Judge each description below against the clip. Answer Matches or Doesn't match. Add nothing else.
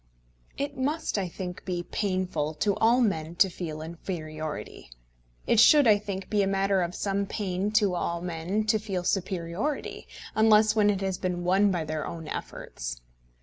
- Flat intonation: Doesn't match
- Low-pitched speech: Doesn't match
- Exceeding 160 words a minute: Matches